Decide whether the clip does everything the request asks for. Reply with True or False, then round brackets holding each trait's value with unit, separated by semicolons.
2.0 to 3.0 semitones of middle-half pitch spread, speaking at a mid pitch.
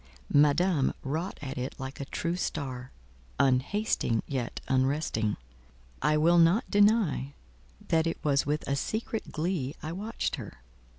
False (4.6 semitones; 150 Hz)